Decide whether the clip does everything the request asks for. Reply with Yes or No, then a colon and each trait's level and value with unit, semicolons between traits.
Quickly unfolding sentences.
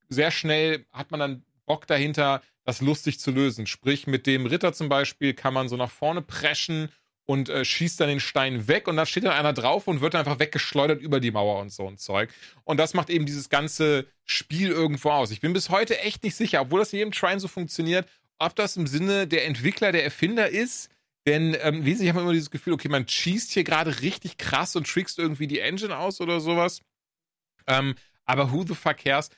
Yes: fast, 225 wpm